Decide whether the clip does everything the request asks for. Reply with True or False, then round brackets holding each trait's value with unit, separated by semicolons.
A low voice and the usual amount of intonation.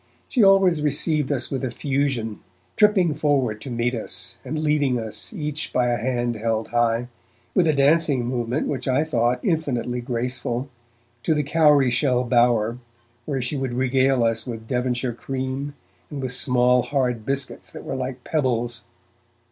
True (130 Hz; 3.2 semitones)